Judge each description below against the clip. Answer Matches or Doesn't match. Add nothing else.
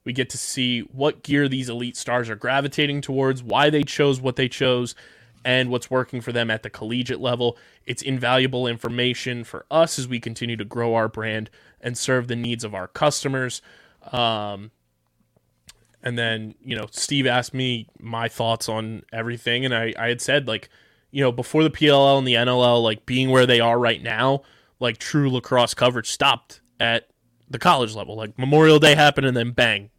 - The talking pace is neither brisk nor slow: Matches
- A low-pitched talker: Matches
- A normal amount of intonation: Doesn't match